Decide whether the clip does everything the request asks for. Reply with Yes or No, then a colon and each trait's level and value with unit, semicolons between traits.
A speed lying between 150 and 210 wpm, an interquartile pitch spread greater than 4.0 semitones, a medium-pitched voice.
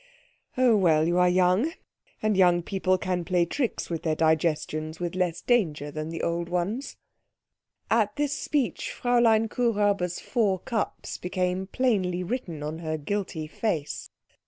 No: average, 140 wpm; average, 4.5 semitones; medium, 180 Hz